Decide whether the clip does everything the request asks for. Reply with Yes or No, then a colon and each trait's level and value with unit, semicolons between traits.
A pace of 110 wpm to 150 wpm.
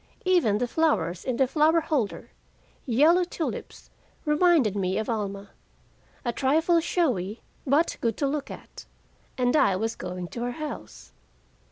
Yes: average, 145 wpm